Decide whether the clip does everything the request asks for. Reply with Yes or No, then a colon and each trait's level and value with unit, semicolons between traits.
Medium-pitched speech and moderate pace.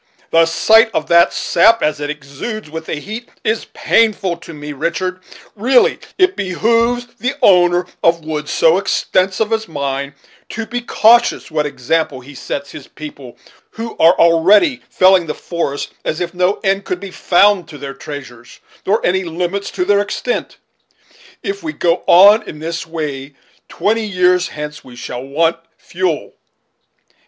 Yes: medium, 175 Hz; average, 160 wpm